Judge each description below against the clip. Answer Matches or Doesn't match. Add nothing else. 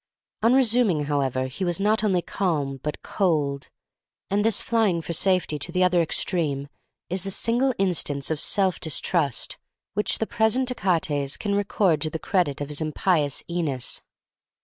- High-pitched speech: Doesn't match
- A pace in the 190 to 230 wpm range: Doesn't match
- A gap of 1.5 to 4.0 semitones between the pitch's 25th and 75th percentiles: Doesn't match